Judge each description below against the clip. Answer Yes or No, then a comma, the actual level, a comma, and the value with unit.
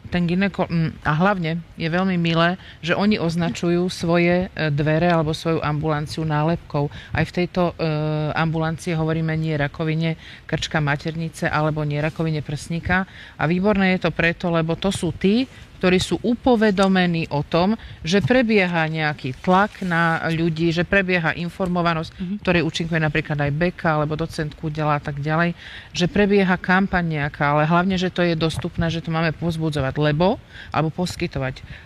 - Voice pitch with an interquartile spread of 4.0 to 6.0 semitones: No, narrow, 2.4 semitones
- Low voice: No, medium, 165 Hz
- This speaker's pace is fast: No, average, 150 wpm